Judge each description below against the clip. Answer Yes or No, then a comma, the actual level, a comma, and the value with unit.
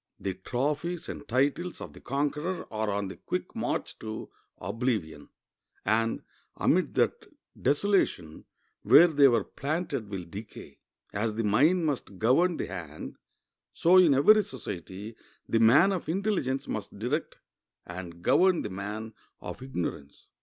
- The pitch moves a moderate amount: No, wide, 7.5 semitones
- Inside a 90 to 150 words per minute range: Yes, average, 140 wpm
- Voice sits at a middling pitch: No, low, 120 Hz